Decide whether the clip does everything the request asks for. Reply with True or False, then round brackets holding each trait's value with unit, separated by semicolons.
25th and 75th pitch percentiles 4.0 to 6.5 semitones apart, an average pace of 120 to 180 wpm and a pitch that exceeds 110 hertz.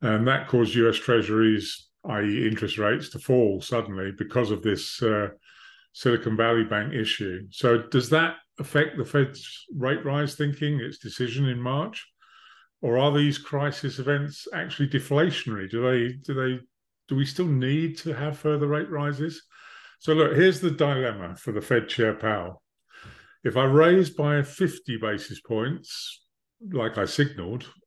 True (5.0 semitones; 155 wpm; 135 Hz)